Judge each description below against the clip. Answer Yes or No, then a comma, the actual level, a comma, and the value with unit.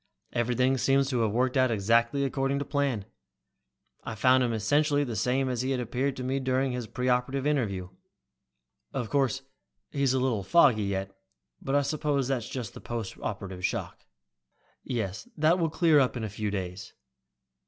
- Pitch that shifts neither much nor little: Yes, average, 3.4 semitones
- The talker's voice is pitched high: No, low, 130 Hz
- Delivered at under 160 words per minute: No, average, 175 wpm